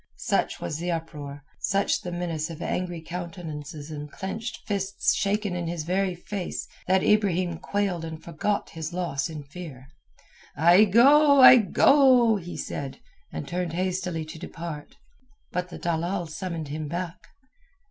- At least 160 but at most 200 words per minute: No, average, 145 wpm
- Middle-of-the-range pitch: Yes, medium, 175 Hz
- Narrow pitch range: No, average, 3.3 semitones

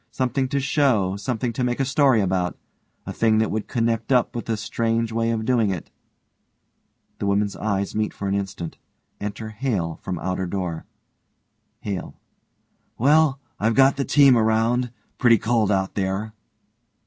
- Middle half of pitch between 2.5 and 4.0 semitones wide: Yes, average, 3.7 semitones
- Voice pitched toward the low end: Yes, low, 110 Hz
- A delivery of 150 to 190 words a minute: Yes, average, 160 wpm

